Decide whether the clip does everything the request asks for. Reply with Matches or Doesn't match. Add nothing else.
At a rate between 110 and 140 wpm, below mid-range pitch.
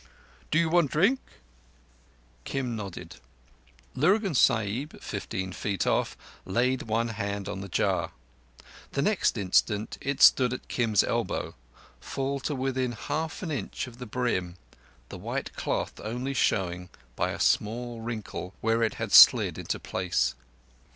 Matches